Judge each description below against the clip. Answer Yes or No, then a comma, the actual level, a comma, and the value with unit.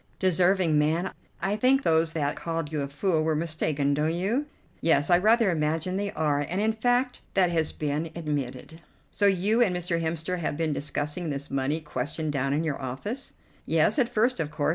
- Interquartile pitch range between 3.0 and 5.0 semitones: Yes, average, 4.3 semitones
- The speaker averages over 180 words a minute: Yes, average, 190 wpm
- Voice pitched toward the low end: No, medium, 165 Hz